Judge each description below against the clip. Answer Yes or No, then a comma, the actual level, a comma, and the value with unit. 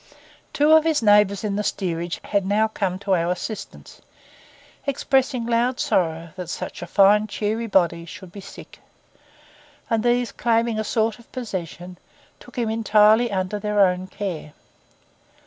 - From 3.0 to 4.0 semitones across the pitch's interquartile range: Yes, average, 3.7 semitones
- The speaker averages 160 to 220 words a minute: No, average, 150 wpm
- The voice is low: No, high, 210 Hz